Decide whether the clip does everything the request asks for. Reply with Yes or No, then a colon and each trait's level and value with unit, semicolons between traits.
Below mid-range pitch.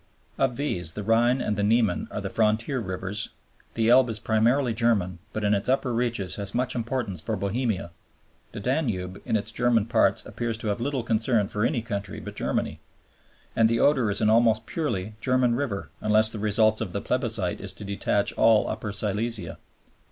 Yes: low, 110 Hz